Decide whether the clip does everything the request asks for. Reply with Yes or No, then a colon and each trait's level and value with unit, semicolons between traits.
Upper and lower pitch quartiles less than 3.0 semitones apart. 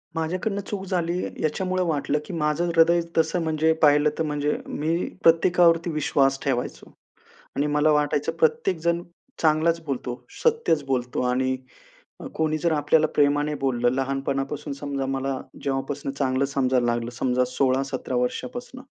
No: average, 3.5 semitones